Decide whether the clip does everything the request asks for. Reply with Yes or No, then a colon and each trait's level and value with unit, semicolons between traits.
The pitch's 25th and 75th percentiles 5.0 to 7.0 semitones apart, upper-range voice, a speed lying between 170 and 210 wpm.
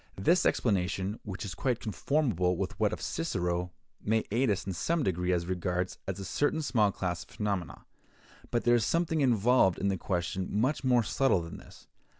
No: average, 5.3 semitones; low, 100 Hz; average, 180 wpm